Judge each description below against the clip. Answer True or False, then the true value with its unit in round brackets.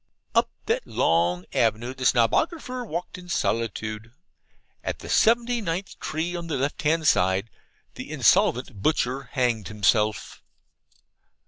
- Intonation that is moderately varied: False (7.9 semitones)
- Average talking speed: False (125 wpm)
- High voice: False (130 Hz)